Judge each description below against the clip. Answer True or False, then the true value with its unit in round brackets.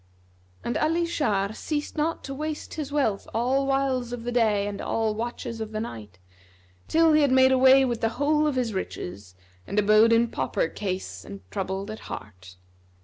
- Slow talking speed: False (190 wpm)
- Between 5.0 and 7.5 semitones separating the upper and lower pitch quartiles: True (5.5 semitones)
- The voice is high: True (230 Hz)